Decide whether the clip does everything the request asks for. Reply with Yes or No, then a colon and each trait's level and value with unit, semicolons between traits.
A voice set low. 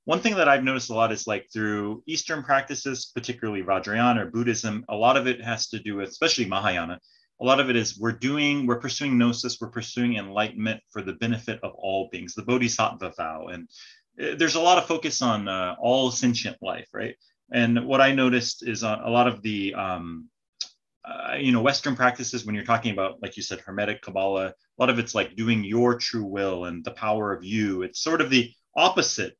Yes: low, 120 Hz